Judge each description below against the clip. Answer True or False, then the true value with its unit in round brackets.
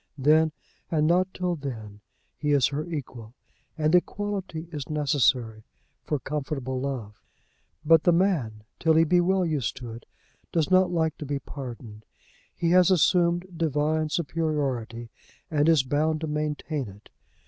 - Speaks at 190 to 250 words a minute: False (150 wpm)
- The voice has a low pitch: False (150 Hz)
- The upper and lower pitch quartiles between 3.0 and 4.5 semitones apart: True (4.1 semitones)